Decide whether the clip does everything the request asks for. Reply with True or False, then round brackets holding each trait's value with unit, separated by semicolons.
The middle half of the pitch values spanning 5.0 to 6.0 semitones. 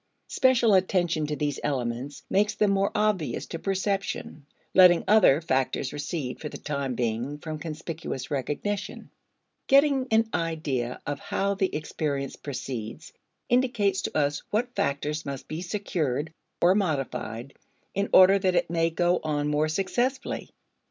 True (5.5 semitones)